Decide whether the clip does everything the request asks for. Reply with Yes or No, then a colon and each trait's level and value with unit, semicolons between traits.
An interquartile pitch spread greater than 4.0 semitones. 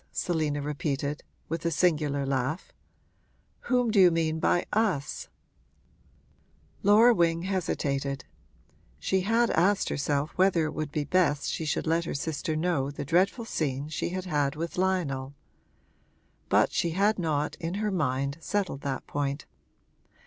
Yes: average, 4.4 semitones